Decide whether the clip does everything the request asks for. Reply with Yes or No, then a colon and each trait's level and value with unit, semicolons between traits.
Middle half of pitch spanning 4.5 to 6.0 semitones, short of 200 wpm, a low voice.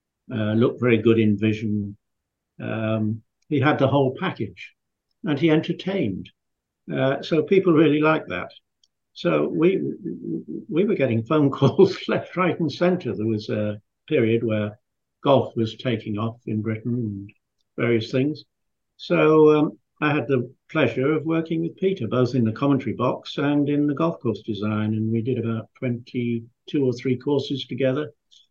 Yes: average, 5.3 semitones; average, 160 wpm; low, 125 Hz